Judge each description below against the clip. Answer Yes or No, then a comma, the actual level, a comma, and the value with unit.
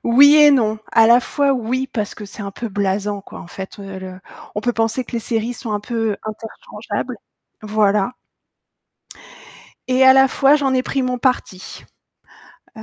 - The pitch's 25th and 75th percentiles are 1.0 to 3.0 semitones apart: No, average, 3.8 semitones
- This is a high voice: Yes, high, 225 Hz